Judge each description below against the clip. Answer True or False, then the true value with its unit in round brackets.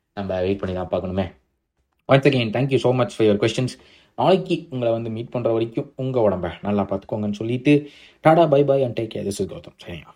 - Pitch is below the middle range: True (115 Hz)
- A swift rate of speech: True (190 wpm)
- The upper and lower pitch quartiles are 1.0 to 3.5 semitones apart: False (5.1 semitones)